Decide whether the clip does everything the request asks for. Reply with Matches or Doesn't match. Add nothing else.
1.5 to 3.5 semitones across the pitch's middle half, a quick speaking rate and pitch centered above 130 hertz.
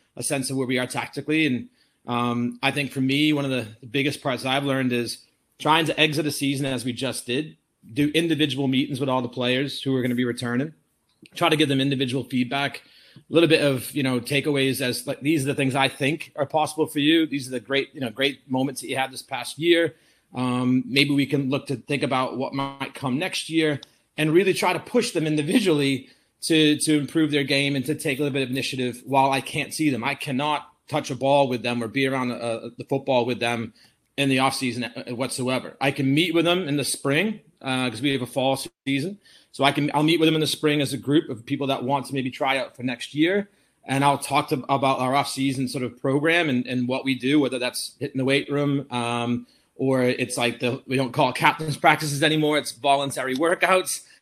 Matches